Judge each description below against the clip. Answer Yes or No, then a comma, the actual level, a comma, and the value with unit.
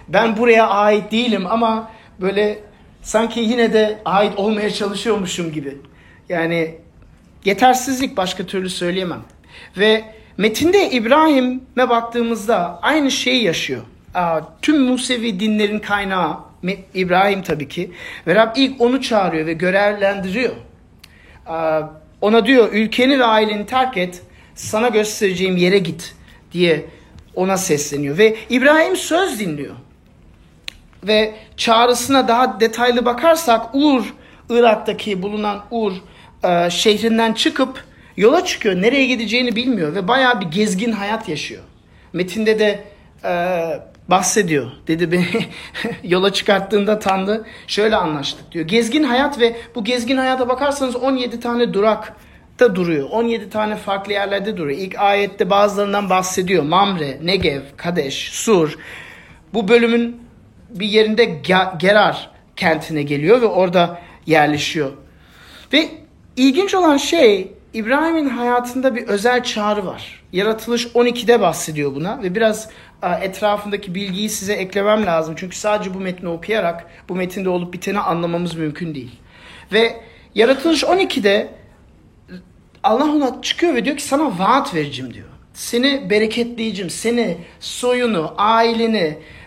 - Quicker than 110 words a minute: Yes, average, 120 wpm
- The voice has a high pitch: Yes, high, 210 Hz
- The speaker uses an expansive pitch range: No, average, 4.7 semitones